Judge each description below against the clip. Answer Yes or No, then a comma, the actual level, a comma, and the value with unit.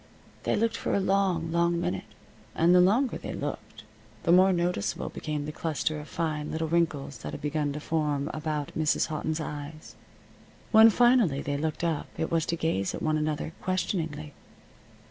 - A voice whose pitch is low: No, medium, 160 Hz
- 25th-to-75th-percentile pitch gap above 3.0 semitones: No, narrow, 2.6 semitones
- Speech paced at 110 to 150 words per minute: No, average, 175 wpm